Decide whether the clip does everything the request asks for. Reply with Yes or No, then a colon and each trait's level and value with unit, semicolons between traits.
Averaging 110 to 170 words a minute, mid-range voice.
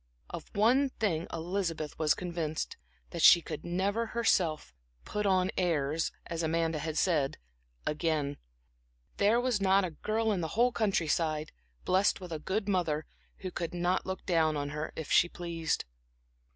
Yes: average, 155 wpm; medium, 175 Hz